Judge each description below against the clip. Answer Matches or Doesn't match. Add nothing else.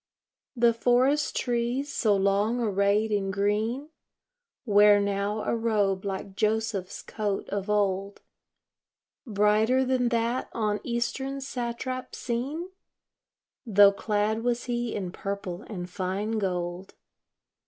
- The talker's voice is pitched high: Matches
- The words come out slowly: Matches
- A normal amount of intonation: Matches